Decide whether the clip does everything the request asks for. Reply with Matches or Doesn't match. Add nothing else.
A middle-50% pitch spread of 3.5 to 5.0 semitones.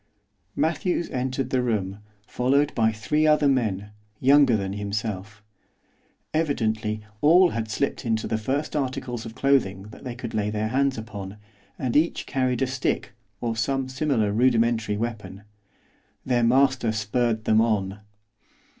Matches